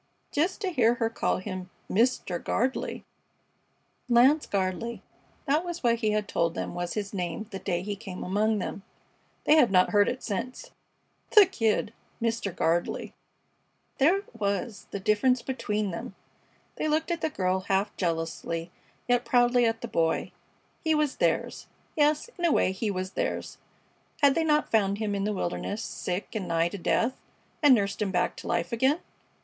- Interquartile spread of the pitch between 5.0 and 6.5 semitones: Yes, wide, 5.6 semitones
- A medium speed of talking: Yes, average, 175 wpm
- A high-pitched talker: Yes, high, 215 Hz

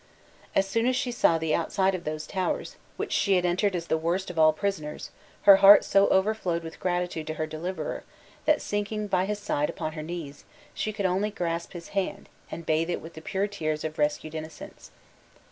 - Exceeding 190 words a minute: Yes, fast, 205 wpm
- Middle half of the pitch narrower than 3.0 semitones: No, average, 3.9 semitones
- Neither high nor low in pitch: Yes, medium, 175 Hz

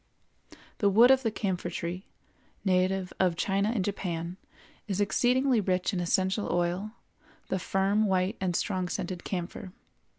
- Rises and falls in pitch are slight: Yes, narrow, 2.2 semitones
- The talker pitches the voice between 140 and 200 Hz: Yes, high, 190 Hz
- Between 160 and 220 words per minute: No, average, 140 wpm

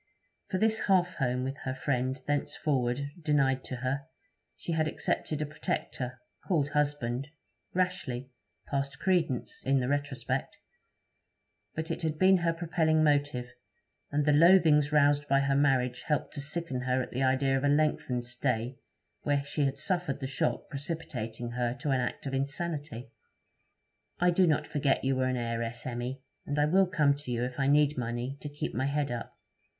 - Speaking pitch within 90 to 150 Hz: Yes, medium, 140 Hz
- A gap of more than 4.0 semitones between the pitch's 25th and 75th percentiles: No, average, 3.0 semitones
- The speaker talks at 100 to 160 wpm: No, average, 175 wpm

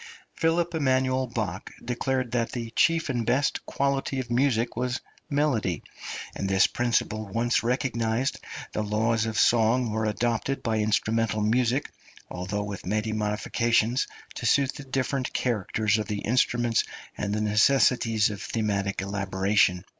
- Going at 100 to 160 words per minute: Yes, average, 140 wpm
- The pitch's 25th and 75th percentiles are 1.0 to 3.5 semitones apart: Yes, average, 3.2 semitones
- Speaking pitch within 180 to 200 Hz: No, low, 115 Hz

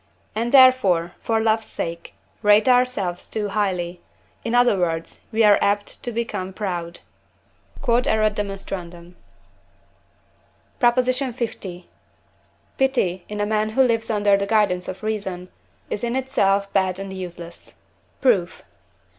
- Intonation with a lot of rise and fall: No, average, 4.0 semitones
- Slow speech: Yes, slow, 120 wpm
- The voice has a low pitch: No, high, 205 Hz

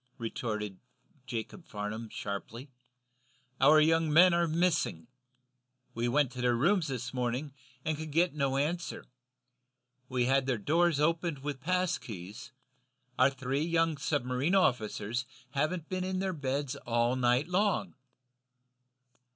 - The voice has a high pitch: No, medium, 140 Hz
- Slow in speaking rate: Yes, slow, 130 wpm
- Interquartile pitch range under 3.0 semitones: No, average, 5.2 semitones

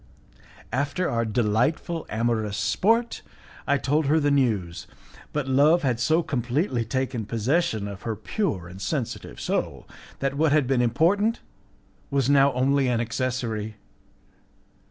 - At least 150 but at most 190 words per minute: No, slow, 135 wpm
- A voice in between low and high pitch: No, low, 130 Hz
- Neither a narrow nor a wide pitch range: Yes, average, 4.8 semitones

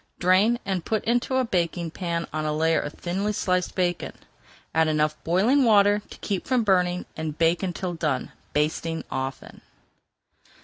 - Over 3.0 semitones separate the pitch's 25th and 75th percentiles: Yes, average, 3.8 semitones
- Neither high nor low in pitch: Yes, medium, 175 Hz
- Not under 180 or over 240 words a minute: No, average, 160 wpm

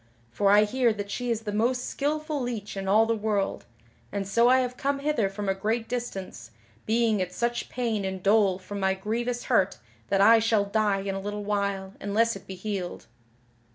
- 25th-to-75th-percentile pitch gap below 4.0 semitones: Yes, average, 3.2 semitones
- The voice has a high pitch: Yes, high, 210 Hz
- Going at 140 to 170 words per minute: No, average, 200 wpm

